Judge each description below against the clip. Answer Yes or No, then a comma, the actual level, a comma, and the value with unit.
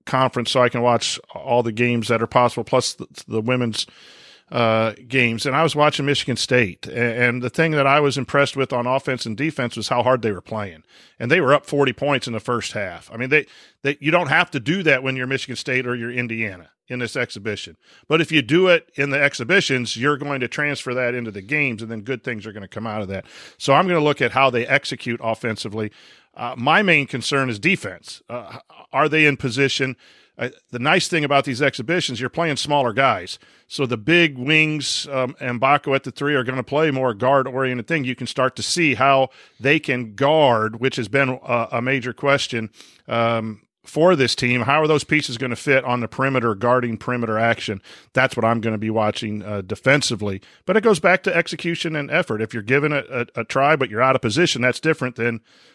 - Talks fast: Yes, fast, 230 wpm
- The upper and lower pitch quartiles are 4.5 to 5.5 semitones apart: No, average, 3.4 semitones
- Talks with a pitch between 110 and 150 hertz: Yes, low, 130 Hz